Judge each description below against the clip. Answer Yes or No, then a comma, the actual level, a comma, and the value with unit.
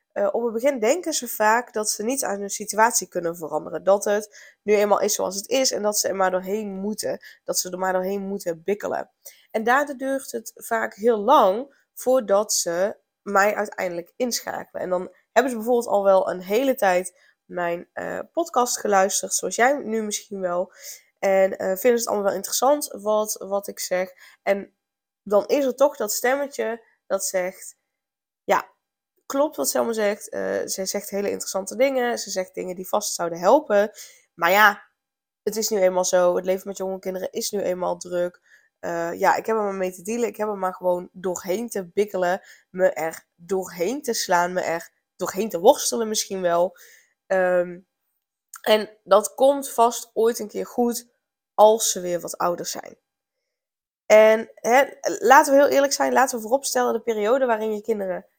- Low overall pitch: No, high, 205 Hz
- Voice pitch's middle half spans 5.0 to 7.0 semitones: No, average, 4.0 semitones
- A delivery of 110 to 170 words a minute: No, average, 185 wpm